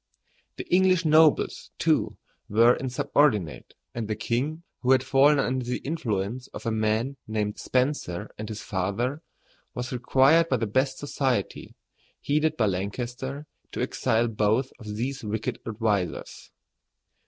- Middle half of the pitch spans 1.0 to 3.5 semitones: No, average, 4.3 semitones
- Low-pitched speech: Yes, low, 125 Hz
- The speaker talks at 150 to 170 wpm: No, slow, 135 wpm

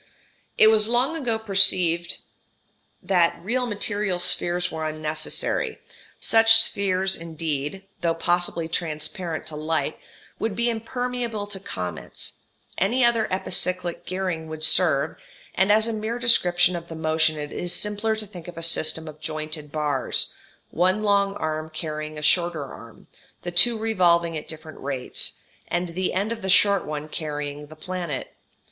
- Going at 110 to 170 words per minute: Yes, average, 150 wpm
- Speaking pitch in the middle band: Yes, medium, 175 Hz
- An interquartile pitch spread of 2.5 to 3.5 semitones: No, average, 4.7 semitones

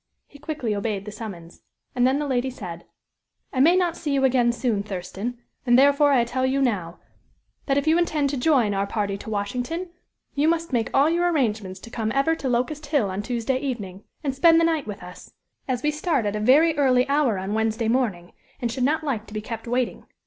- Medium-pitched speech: No, very high, 250 Hz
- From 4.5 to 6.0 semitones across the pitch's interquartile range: Yes, average, 5.2 semitones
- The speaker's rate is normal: No, fast, 220 wpm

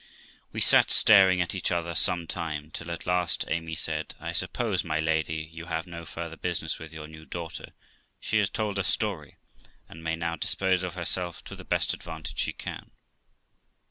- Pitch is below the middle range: Yes, very low, 85 Hz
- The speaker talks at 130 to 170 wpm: No, average, 185 wpm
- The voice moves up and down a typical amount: No, narrow, 2.1 semitones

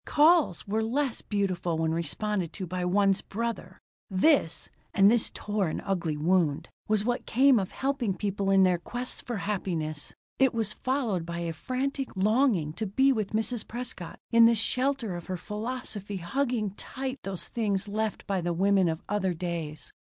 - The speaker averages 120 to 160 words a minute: No, average, 170 wpm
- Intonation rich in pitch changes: No, average, 4.9 semitones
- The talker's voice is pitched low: No, high, 205 Hz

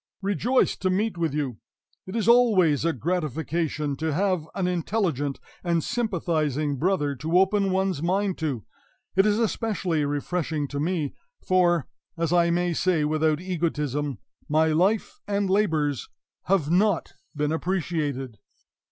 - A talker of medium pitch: Yes, medium, 170 Hz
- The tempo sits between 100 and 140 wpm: Yes, slow, 135 wpm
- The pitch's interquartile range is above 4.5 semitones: No, average, 4.1 semitones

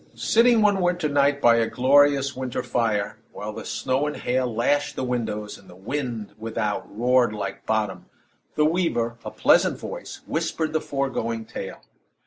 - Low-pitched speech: Yes, low, 130 Hz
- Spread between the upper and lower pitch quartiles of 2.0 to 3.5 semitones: No, average, 4.2 semitones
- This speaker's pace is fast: No, average, 160 wpm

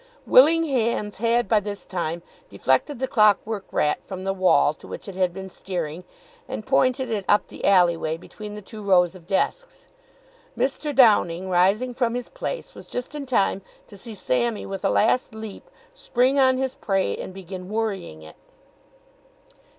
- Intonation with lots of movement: No, average, 4.9 semitones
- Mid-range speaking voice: No, high, 210 Hz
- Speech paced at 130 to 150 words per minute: No, average, 175 wpm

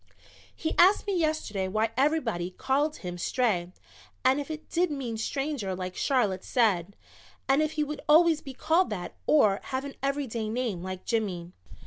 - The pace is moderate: Yes, average, 165 wpm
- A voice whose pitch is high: Yes, very high, 255 Hz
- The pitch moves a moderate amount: No, wide, 7.5 semitones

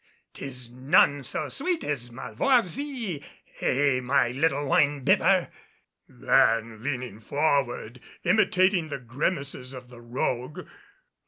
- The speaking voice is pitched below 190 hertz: Yes, low, 135 Hz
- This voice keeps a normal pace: No, slow, 105 wpm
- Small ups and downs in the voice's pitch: No, average, 4.4 semitones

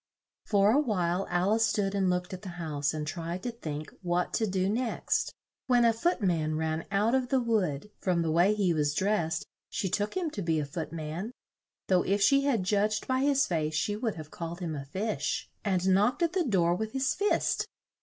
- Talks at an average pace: No, fast, 215 wpm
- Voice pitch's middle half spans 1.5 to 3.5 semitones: No, average, 4.9 semitones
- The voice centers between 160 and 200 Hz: Yes, high, 190 Hz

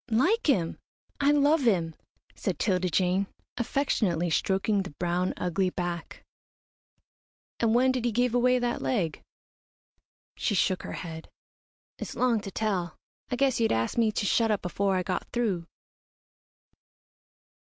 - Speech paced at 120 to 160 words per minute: Yes, average, 140 wpm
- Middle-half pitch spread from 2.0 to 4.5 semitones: No, average, 5.2 semitones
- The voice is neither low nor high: No, high, 205 Hz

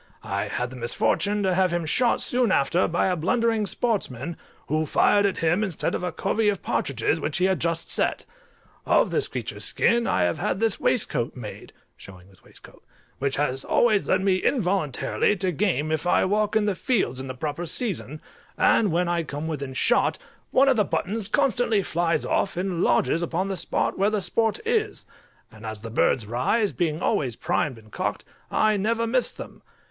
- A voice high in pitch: No, medium, 180 Hz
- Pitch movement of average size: No, wide, 6.3 semitones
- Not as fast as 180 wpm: No, average, 190 wpm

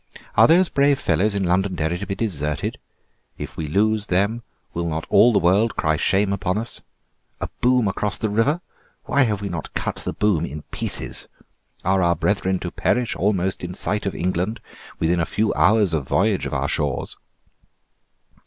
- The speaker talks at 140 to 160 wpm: No, average, 175 wpm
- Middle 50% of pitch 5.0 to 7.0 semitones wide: No, average, 3.8 semitones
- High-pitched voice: No, low, 100 Hz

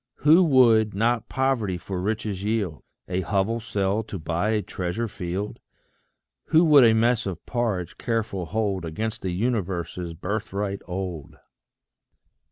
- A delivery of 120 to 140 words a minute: Yes, slow, 135 wpm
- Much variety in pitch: No, average, 3.8 semitones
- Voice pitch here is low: Yes, low, 105 Hz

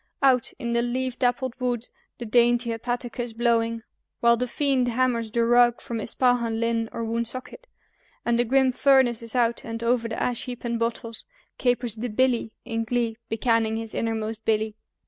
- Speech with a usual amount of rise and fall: No, narrow, 1.3 semitones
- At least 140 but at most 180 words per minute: Yes, average, 170 wpm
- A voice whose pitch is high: Yes, high, 235 Hz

